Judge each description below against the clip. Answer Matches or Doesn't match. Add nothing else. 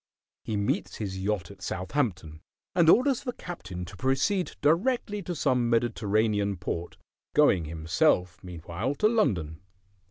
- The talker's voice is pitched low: Matches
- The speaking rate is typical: Doesn't match